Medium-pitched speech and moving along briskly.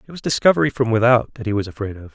No: low, 120 Hz; fast, 280 wpm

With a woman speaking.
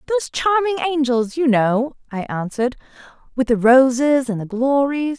Yes: female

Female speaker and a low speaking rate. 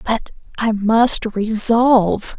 Yes: female; slow, 100 wpm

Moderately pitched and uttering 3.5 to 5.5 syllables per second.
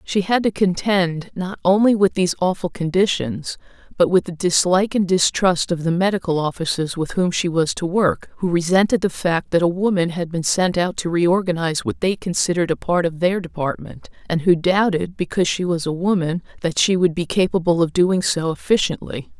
Yes: medium, 180 Hz; 5.3 syllables/s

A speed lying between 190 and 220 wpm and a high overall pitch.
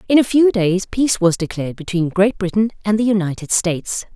Yes: average, 200 wpm; high, 195 Hz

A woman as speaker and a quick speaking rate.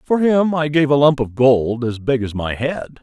No: male; fast, 260 wpm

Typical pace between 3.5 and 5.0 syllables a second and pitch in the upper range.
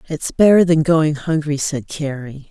No: 4.3 syllables/s; medium, 150 Hz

